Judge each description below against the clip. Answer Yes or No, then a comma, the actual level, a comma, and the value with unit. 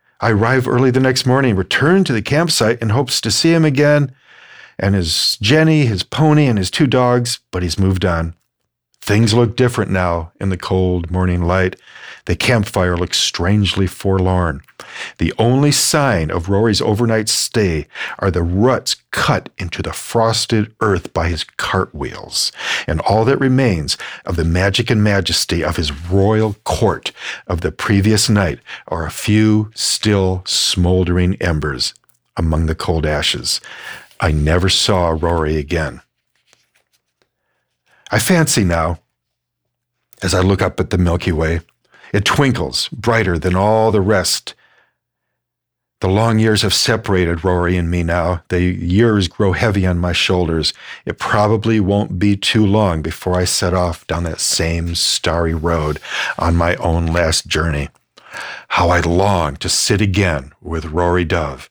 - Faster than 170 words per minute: No, average, 155 wpm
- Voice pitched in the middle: No, very low, 95 Hz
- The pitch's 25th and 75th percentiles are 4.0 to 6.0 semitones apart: Yes, average, 4.5 semitones